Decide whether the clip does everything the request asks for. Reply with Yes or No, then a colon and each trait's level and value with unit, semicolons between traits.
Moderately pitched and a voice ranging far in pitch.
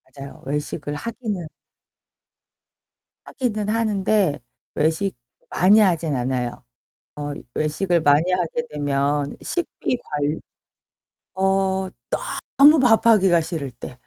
Yes: medium, 175 Hz; wide, 6.1 semitones